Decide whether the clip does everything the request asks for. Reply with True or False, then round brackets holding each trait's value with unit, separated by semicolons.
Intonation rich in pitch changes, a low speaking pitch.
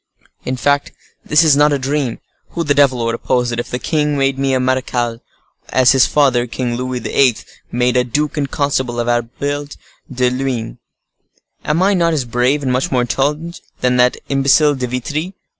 False (2.7 semitones; 130 Hz)